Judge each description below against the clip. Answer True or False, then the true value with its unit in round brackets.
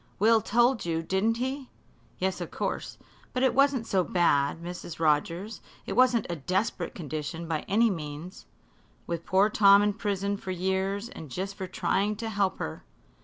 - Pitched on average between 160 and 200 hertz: True (190 Hz)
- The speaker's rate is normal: True (170 wpm)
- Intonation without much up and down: False (4.4 semitones)